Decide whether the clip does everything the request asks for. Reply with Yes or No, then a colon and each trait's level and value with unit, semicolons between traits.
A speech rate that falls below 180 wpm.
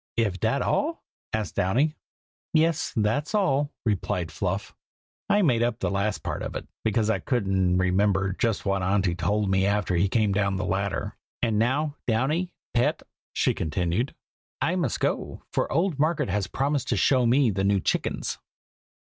Yes: average, 165 wpm